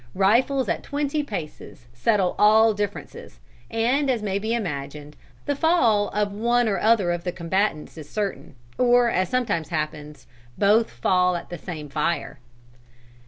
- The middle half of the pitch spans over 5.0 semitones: Yes, wide, 5.5 semitones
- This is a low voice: No, high, 205 Hz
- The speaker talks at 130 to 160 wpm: Yes, average, 150 wpm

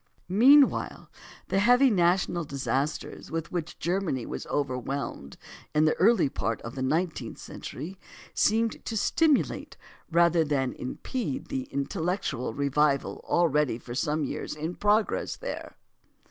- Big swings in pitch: Yes, wide, 6.1 semitones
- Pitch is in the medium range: Yes, medium, 160 Hz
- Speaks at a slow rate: Yes, slow, 125 wpm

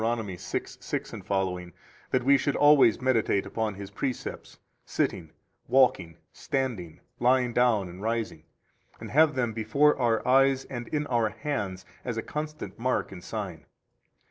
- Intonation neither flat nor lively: Yes, average, 4.7 semitones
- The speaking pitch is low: Yes, low, 120 Hz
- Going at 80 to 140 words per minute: Yes, slow, 135 wpm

